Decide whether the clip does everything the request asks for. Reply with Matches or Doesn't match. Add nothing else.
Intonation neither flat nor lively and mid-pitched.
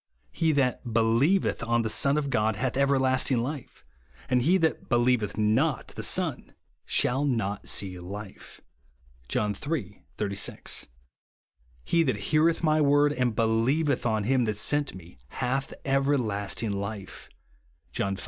Doesn't match